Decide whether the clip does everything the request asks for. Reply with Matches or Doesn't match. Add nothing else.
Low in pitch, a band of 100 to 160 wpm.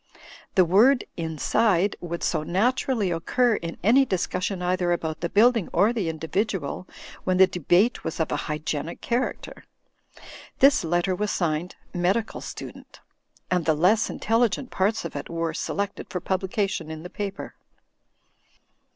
Doesn't match